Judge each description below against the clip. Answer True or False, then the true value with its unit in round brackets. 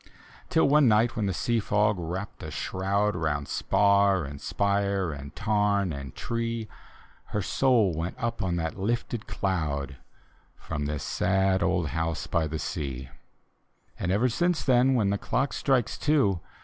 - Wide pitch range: True (5.7 semitones)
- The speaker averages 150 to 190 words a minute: True (155 wpm)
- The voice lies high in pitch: False (100 Hz)